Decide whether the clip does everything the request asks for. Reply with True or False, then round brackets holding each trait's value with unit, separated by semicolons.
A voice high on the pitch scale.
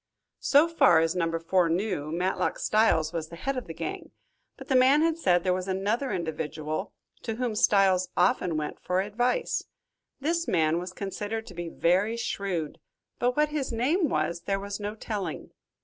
True (195 Hz)